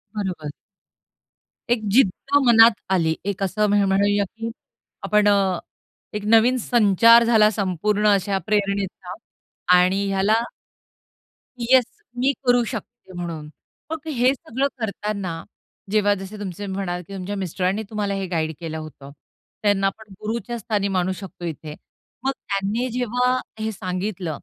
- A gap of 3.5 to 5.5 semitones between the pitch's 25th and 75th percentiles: No, average, 3.1 semitones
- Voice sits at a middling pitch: No, high, 200 Hz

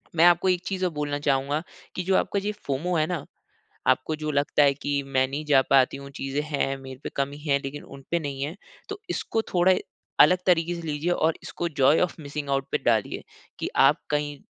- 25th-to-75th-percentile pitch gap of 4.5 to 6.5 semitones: No, average, 3.7 semitones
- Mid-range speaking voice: Yes, medium, 145 Hz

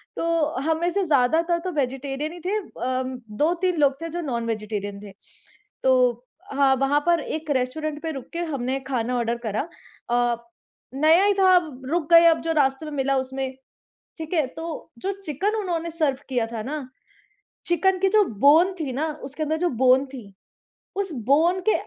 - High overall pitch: Yes, very high, 295 Hz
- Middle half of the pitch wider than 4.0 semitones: Yes, average, 4.6 semitones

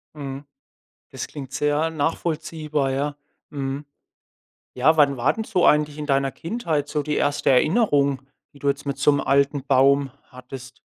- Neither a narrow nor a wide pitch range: No, narrow, 1.8 semitones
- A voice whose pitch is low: No, medium, 145 Hz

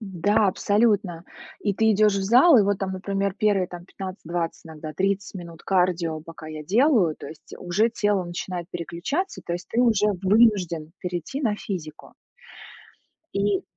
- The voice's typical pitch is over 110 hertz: Yes, high, 190 Hz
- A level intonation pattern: No, average, 3.3 semitones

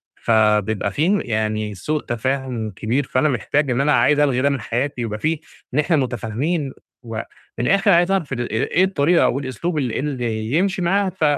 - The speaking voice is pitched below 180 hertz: Yes, low, 135 Hz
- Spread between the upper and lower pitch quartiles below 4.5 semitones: No, wide, 5.5 semitones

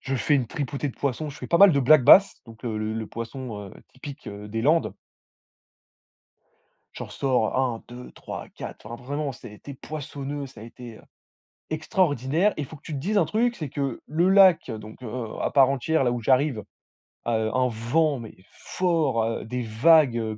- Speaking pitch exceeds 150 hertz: No, low, 135 Hz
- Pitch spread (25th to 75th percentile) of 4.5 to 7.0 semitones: Yes, average, 4.9 semitones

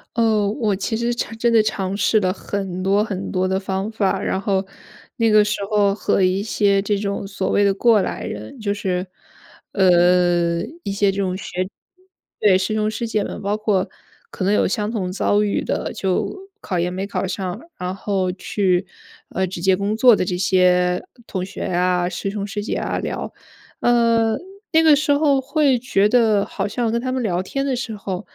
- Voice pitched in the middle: No, high, 200 Hz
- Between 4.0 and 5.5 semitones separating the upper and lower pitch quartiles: No, average, 2.9 semitones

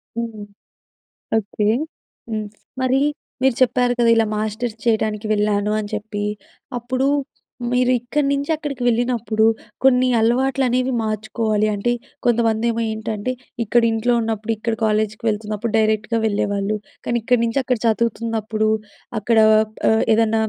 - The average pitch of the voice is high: Yes, high, 225 Hz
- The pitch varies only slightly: Yes, narrow, 2.1 semitones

